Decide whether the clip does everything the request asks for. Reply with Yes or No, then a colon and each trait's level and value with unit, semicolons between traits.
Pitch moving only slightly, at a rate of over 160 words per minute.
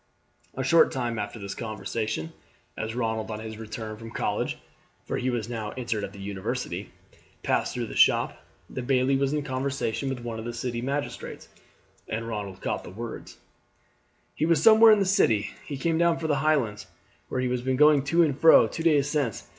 No: average, 4.7 semitones; average, 195 wpm